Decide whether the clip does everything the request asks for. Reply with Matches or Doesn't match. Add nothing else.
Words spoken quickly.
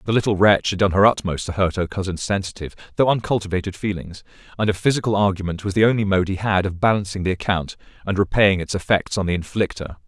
Matches